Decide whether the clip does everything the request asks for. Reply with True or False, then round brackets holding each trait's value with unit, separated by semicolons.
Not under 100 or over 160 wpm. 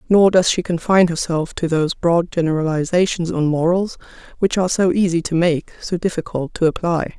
False (175 wpm)